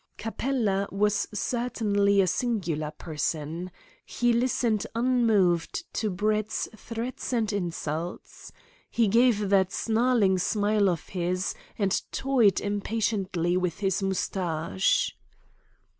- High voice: Yes, high, 200 Hz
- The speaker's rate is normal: No, slow, 100 wpm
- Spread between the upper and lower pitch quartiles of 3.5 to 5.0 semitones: Yes, average, 3.8 semitones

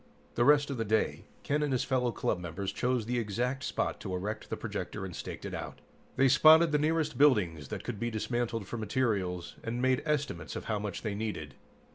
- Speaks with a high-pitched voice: No, low, 115 Hz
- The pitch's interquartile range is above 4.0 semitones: Yes, average, 5.0 semitones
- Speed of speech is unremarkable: No, fast, 210 wpm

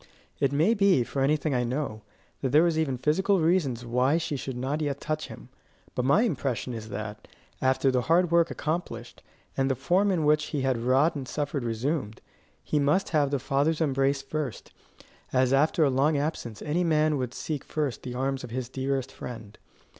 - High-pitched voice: No, medium, 140 Hz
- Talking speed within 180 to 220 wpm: Yes, average, 190 wpm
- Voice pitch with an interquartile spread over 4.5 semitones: No, average, 3.3 semitones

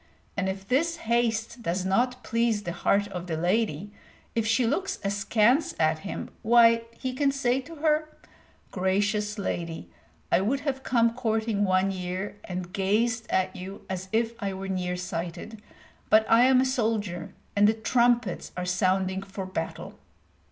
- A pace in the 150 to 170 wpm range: Yes, average, 160 wpm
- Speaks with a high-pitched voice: Yes, high, 210 Hz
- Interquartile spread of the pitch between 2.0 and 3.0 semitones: No, average, 3.9 semitones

